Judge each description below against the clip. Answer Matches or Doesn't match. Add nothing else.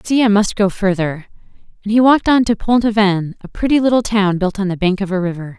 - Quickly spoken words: Matches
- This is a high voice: Matches